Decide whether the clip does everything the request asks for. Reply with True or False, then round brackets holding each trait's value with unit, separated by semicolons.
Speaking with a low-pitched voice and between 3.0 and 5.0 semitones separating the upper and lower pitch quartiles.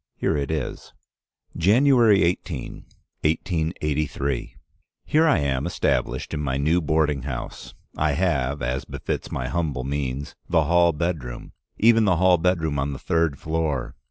True (80 Hz; 4.0 semitones)